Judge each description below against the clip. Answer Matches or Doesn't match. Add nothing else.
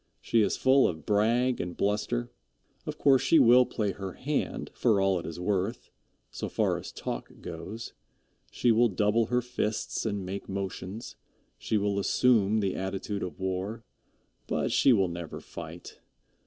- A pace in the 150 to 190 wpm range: Matches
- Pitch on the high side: Doesn't match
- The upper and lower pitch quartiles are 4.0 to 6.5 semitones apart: Doesn't match